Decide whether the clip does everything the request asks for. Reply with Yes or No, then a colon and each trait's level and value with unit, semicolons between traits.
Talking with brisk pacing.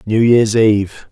No: average, 160 wpm